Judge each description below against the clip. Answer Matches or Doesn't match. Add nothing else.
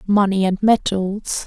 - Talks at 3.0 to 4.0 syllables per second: Matches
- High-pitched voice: Matches